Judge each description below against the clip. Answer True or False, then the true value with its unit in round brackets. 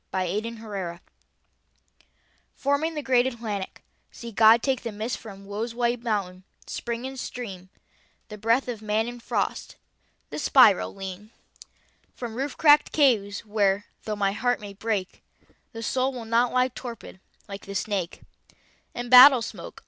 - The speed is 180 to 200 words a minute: False (150 wpm)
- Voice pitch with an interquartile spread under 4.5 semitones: True (3.5 semitones)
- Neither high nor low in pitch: False (225 Hz)